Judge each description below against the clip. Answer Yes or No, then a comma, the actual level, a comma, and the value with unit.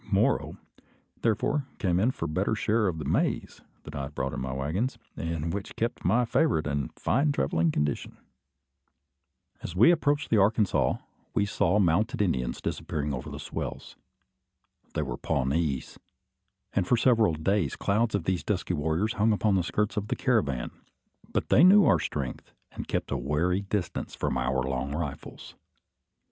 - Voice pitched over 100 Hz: No, very low, 90 Hz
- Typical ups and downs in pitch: No, wide, 6.7 semitones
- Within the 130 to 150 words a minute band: No, average, 170 wpm